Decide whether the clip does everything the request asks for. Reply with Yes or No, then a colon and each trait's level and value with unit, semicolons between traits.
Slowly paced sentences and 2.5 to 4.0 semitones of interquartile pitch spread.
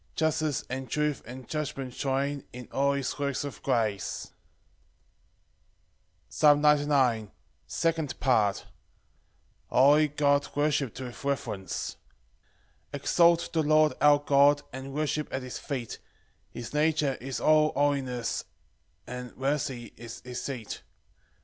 Yes: slow, 120 wpm; average, 2.9 semitones